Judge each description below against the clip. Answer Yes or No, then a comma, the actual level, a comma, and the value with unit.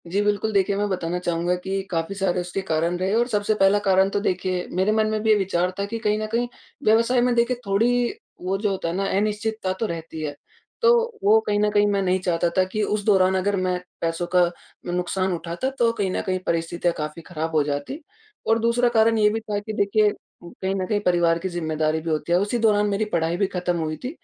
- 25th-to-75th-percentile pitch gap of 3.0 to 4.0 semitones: Yes, average, 3.5 semitones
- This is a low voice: No, high, 195 Hz